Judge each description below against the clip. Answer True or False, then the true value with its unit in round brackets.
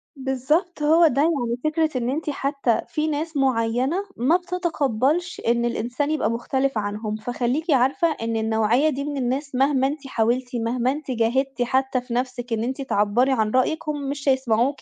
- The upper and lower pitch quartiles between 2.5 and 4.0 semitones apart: True (3.7 semitones)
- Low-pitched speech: False (265 Hz)